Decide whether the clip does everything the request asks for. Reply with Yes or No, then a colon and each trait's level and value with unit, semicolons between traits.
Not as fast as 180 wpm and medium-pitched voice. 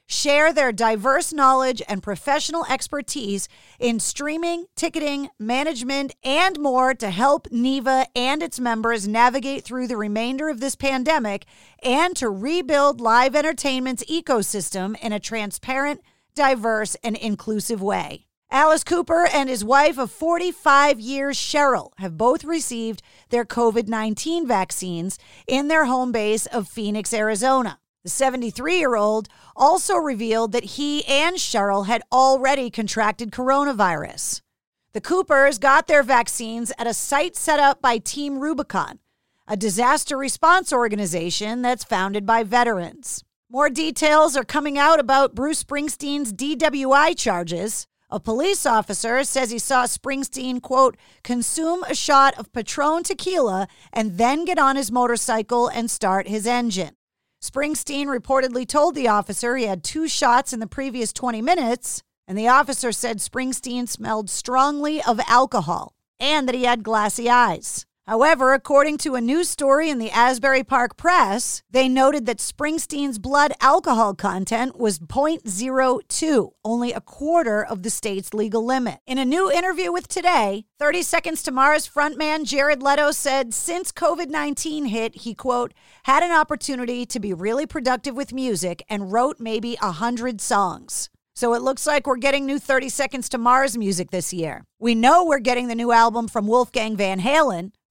No: average, 150 wpm; very high, 260 Hz